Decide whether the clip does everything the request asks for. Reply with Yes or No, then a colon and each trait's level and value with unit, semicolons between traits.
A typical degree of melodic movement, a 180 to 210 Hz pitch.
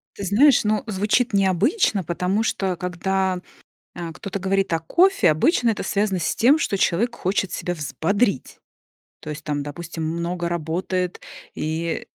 Yes: average, 3.5 semitones; medium, 185 Hz